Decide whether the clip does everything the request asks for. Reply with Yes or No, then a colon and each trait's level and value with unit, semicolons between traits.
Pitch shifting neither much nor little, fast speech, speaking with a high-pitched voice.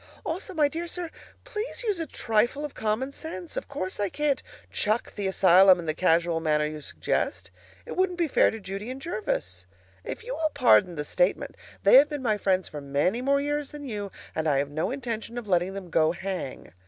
No: wide, 8.5 semitones; fast, 210 wpm; high, 210 Hz